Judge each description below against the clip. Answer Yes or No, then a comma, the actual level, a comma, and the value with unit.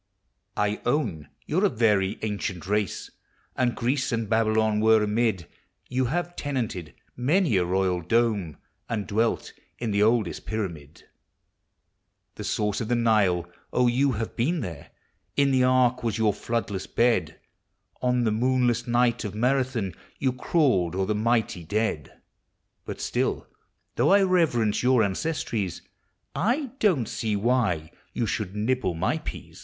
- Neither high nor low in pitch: No, low, 115 Hz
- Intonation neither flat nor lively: Yes, average, 3.7 semitones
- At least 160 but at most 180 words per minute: No, average, 150 wpm